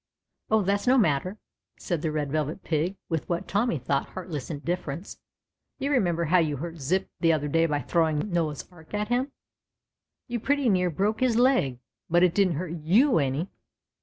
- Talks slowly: No, average, 190 wpm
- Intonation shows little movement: No, average, 5.0 semitones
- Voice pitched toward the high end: No, medium, 170 Hz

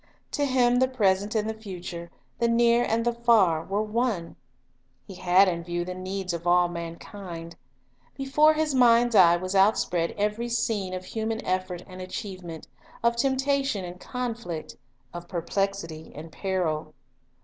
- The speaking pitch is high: Yes, high, 195 Hz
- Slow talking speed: No, average, 160 wpm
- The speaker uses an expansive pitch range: No, average, 5.0 semitones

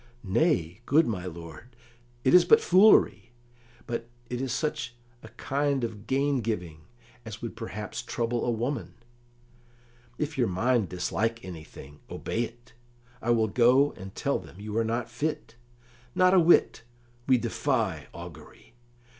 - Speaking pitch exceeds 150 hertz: No, low, 120 Hz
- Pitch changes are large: No, average, 4.3 semitones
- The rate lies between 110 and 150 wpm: Yes, average, 145 wpm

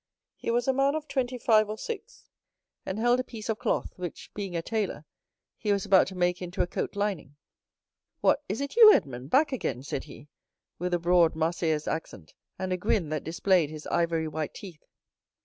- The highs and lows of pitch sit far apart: Yes, wide, 5.8 semitones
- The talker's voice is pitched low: No, medium, 185 Hz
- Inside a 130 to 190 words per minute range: No, average, 200 wpm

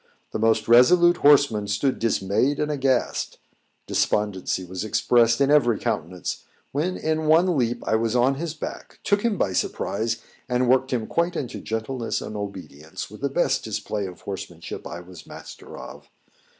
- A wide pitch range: Yes, wide, 5.9 semitones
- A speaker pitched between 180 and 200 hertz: No, low, 120 Hz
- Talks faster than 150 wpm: Yes, average, 165 wpm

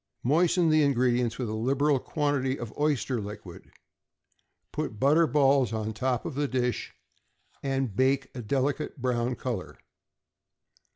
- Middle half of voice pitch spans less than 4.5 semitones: Yes, average, 3.1 semitones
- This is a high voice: No, low, 130 Hz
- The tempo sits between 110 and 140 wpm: Yes, slow, 135 wpm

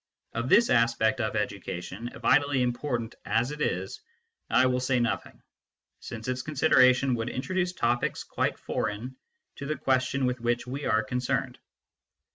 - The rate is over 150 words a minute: No, average, 145 wpm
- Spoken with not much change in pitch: Yes, narrow, 2.3 semitones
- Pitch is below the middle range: Yes, low, 125 Hz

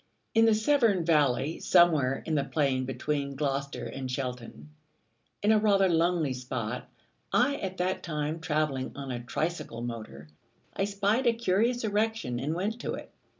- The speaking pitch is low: No, medium, 155 Hz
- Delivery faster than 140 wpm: Yes, average, 155 wpm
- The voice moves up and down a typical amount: No, wide, 7.4 semitones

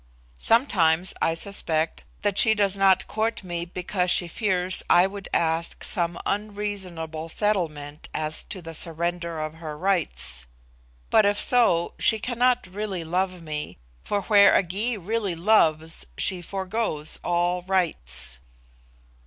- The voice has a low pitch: No, medium, 180 Hz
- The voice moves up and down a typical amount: Yes, average, 3.8 semitones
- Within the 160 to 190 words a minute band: No, slow, 135 wpm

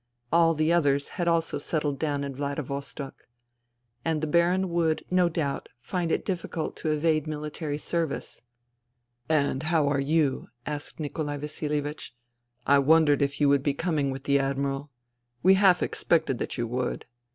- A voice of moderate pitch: Yes, medium, 150 Hz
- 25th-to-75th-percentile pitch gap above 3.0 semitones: No, narrow, 2.6 semitones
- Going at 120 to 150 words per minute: No, average, 160 wpm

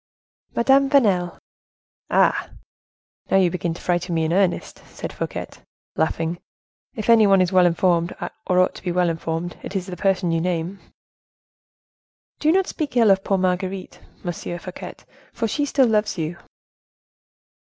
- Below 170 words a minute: Yes, average, 155 wpm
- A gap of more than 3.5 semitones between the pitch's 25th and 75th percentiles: No, average, 3.2 semitones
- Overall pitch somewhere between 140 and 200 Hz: Yes, medium, 185 Hz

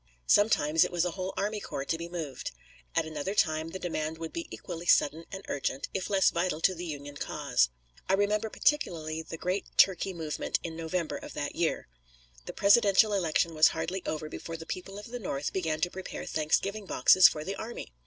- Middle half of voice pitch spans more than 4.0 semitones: No, average, 3.6 semitones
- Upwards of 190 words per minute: Yes, average, 200 wpm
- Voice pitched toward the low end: No, medium, 170 Hz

